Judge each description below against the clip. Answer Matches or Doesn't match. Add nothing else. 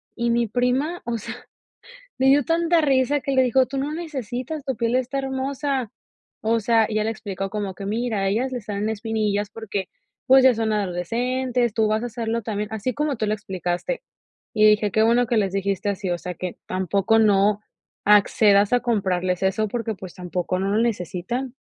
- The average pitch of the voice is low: Doesn't match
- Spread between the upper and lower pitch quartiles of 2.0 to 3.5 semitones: Doesn't match